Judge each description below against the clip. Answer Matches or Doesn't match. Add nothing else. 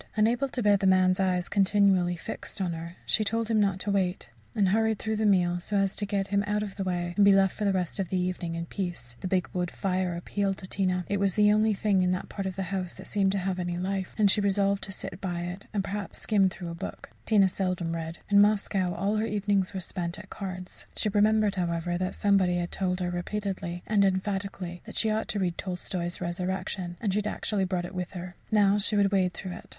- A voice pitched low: Doesn't match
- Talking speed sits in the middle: Doesn't match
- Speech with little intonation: Matches